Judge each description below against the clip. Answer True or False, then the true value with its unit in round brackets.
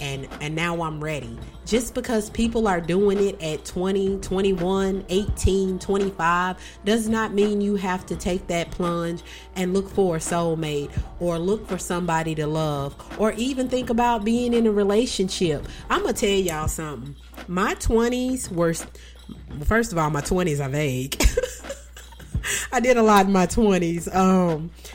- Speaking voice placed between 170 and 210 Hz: True (185 Hz)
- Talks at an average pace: True (165 wpm)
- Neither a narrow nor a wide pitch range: True (4.4 semitones)